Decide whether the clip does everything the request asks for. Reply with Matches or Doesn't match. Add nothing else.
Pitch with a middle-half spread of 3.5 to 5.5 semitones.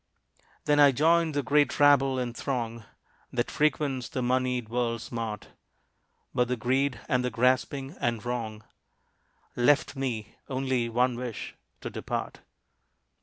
Doesn't match